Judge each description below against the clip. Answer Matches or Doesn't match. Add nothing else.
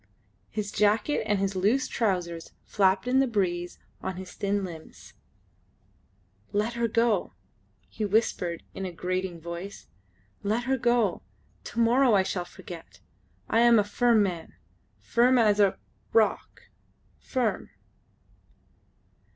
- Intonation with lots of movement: Doesn't match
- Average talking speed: Doesn't match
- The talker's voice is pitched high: Matches